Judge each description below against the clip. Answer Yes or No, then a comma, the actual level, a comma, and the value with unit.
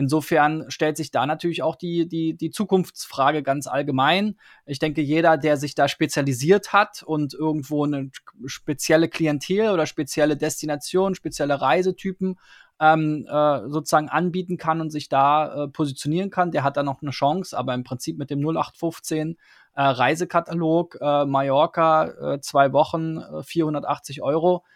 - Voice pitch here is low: No, medium, 155 Hz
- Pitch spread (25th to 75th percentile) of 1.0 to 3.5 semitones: Yes, narrow, 2.5 semitones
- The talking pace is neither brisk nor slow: Yes, average, 150 wpm